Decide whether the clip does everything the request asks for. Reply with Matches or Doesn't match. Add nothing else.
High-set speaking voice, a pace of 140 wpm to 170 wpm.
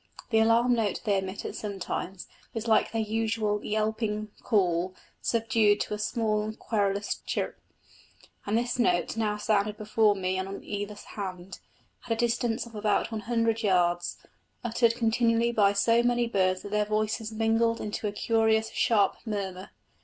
Matches